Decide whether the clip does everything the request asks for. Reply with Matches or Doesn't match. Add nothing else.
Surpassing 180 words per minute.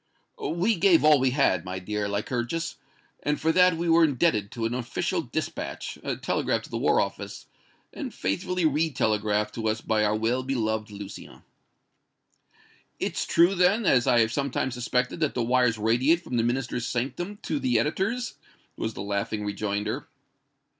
Doesn't match